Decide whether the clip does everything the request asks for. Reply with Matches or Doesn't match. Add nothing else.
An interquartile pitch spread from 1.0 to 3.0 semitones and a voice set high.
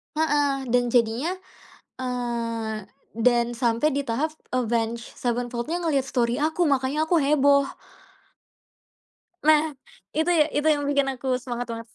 Doesn't match